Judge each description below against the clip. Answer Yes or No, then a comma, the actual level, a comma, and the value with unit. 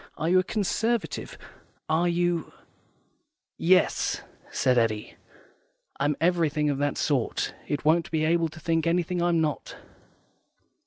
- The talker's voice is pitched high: No, medium, 165 Hz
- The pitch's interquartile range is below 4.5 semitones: Yes, average, 2.7 semitones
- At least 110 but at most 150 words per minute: Yes, average, 145 wpm